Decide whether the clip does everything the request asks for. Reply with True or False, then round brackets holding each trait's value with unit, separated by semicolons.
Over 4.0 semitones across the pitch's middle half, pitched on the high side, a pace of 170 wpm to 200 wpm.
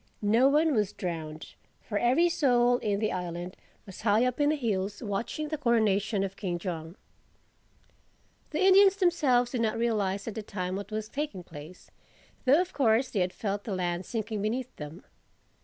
True (5.1 semitones; 215 Hz; 175 wpm)